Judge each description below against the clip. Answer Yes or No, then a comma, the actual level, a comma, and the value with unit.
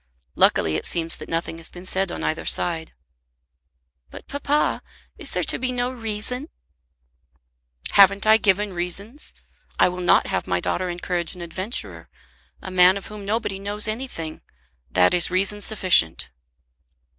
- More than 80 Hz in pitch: Yes, high, 190 Hz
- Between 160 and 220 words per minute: No, average, 150 wpm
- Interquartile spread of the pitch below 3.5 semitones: No, average, 3.8 semitones